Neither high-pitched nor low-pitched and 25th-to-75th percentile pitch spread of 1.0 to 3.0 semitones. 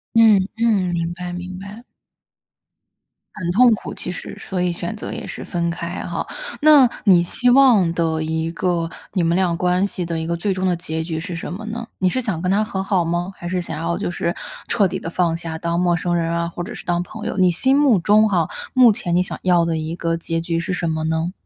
Yes: medium, 175 Hz; average, 2.7 semitones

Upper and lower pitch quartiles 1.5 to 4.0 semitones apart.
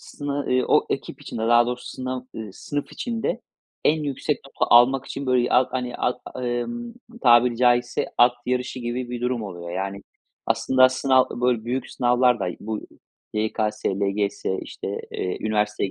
Yes: average, 2.7 semitones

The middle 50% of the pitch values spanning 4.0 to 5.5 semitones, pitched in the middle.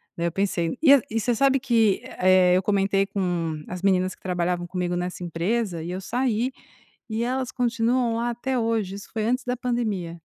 No: average, 4.9 semitones; high, 200 Hz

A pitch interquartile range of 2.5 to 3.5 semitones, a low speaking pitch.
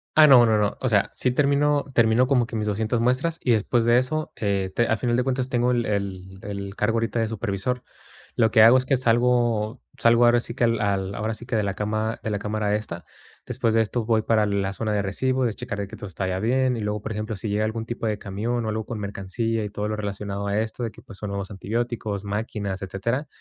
Yes: average, 2.8 semitones; low, 110 Hz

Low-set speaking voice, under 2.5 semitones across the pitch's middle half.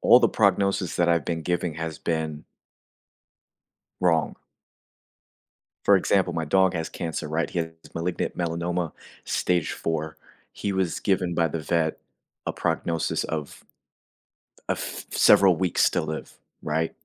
Yes: very low, 85 Hz; narrow, 1.9 semitones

